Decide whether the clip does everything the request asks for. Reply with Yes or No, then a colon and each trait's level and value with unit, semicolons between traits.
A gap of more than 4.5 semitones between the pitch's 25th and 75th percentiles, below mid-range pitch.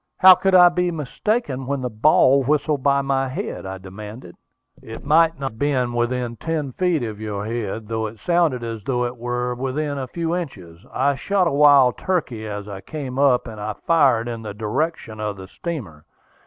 Yes: wide, 5.5 semitones; low, 130 Hz